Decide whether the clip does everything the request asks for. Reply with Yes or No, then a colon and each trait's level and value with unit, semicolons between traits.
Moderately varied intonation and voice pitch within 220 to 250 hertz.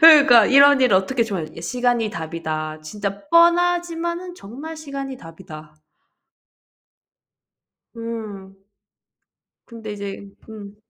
No: wide, 6.6 semitones; high, 230 Hz